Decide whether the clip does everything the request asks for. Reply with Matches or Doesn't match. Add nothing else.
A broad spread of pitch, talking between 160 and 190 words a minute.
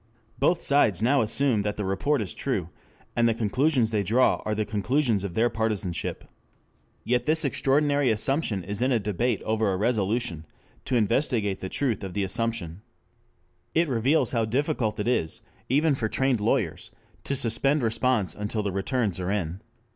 Doesn't match